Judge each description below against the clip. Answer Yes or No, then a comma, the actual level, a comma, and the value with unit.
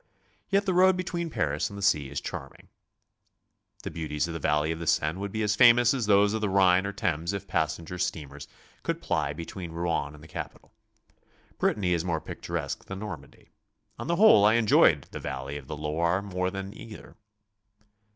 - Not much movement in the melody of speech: No, average, 5.1 semitones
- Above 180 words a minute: Yes, average, 195 wpm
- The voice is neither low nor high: No, very low, 90 Hz